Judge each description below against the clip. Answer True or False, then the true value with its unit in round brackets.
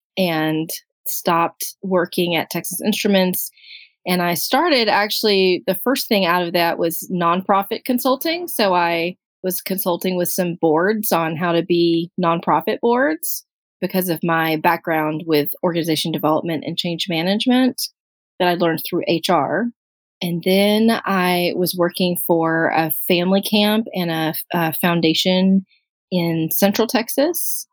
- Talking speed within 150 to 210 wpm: False (135 wpm)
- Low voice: False (180 Hz)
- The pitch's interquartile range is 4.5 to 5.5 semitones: False (3.4 semitones)